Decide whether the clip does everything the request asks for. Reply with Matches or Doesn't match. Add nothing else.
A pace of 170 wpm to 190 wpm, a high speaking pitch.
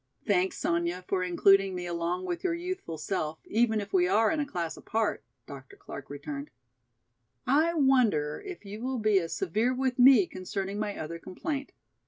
Matches